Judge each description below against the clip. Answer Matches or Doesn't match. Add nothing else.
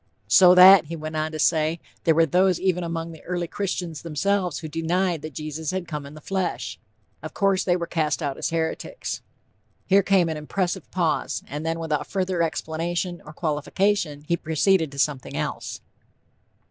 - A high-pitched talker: Doesn't match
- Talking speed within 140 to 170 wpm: Doesn't match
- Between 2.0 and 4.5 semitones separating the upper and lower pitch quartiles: Matches